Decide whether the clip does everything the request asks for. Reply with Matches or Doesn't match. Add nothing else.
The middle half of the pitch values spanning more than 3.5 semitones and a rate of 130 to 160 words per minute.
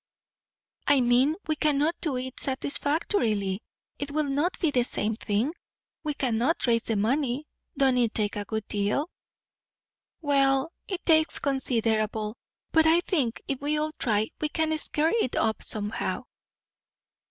Matches